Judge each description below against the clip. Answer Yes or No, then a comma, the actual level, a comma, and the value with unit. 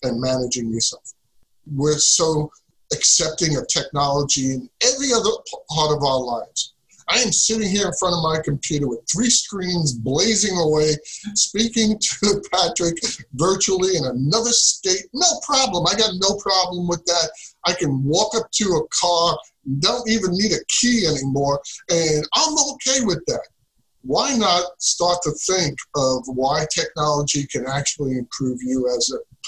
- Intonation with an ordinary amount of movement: No, wide, 6.3 semitones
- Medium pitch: Yes, medium, 170 Hz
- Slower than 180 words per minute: Yes, average, 155 wpm